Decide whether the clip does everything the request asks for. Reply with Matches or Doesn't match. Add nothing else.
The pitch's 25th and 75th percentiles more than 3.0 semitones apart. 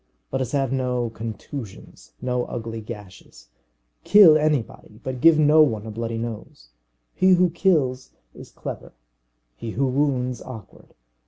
Matches